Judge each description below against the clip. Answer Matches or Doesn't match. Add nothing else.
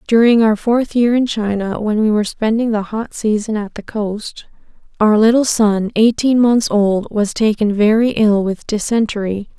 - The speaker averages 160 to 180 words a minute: Matches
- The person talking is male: Doesn't match